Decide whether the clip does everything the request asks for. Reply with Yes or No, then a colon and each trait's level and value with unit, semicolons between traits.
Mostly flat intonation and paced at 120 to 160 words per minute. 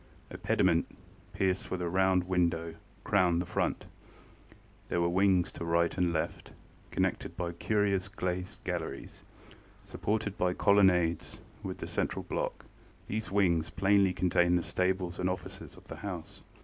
Yes: narrow, 1.9 semitones; average, 145 wpm